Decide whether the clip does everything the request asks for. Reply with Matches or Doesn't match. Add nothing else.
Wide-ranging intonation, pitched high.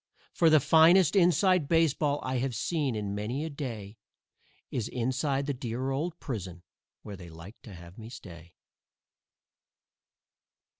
Doesn't match